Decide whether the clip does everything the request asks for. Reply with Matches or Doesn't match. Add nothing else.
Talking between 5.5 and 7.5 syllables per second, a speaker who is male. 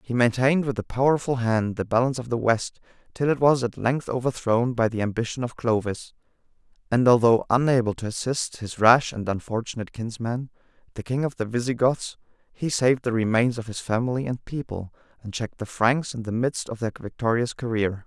Matches